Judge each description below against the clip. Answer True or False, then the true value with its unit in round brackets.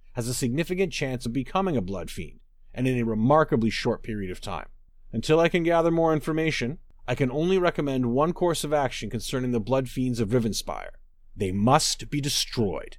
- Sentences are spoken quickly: False (190 wpm)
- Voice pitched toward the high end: False (130 Hz)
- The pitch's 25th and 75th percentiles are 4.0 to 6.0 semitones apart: True (5.1 semitones)